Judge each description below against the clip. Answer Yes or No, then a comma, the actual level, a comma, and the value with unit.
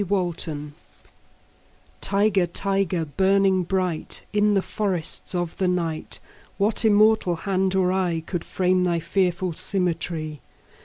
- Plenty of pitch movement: No, narrow, 2.4 semitones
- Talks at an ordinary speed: No, slow, 120 wpm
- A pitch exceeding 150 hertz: Yes, medium, 185 Hz